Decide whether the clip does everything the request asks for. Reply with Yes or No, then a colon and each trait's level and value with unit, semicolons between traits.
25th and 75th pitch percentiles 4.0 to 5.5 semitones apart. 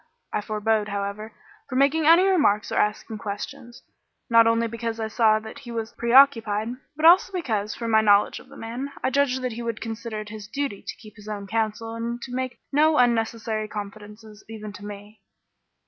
No: average, 2.7 semitones